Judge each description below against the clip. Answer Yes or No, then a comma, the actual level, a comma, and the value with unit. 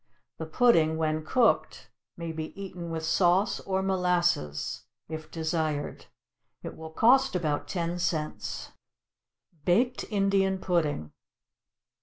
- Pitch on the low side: No, medium, 170 Hz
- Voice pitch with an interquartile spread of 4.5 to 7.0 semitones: No, average, 3.3 semitones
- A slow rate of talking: Yes, slow, 110 wpm